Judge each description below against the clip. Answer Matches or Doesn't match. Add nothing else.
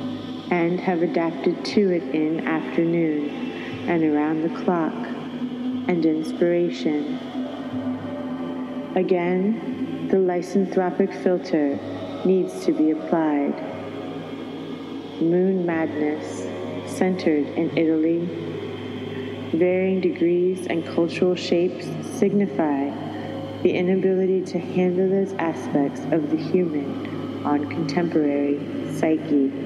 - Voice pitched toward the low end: Doesn't match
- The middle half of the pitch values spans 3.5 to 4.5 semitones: Matches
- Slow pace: Matches